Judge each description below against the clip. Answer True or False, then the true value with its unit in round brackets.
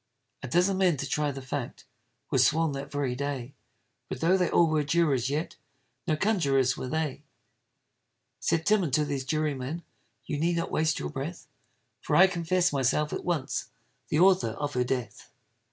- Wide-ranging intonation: False (4.0 semitones)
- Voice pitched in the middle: True (150 Hz)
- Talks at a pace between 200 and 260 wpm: False (170 wpm)